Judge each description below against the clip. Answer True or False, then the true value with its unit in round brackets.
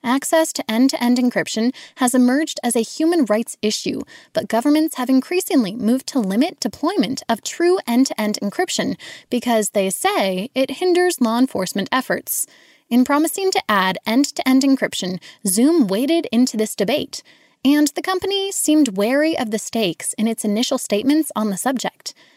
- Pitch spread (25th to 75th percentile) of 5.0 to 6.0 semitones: True (5.6 semitones)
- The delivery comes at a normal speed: True (170 wpm)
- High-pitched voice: True (260 Hz)